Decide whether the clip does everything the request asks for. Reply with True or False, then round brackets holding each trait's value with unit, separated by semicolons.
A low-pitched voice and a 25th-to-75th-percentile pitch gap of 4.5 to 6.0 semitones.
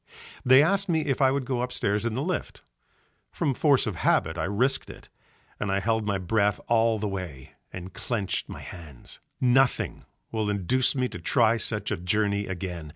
True (110 Hz; 5.2 semitones)